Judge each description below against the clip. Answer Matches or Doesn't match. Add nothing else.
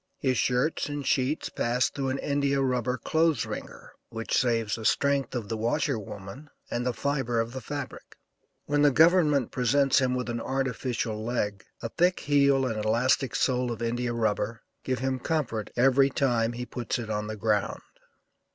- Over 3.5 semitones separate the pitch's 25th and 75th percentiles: Doesn't match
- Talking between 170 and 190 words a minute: Matches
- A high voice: Doesn't match